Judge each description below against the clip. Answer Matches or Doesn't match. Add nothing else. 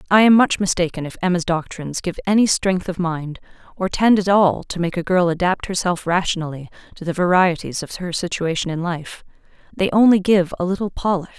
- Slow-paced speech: Doesn't match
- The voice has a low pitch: Doesn't match